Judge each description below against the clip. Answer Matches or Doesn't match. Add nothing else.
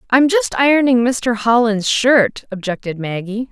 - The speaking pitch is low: Doesn't match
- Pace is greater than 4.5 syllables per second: Doesn't match